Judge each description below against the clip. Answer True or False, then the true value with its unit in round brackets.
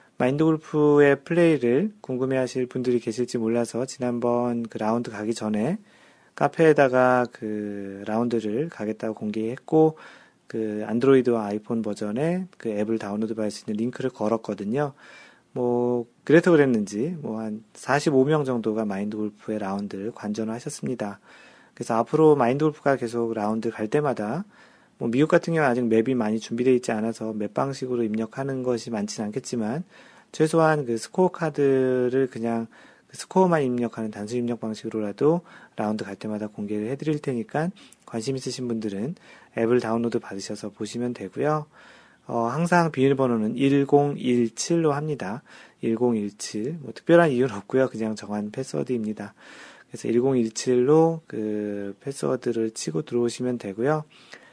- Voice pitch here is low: True (120 Hz)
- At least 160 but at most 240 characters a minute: False (335 characters per minute)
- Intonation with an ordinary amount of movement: True (4.1 semitones)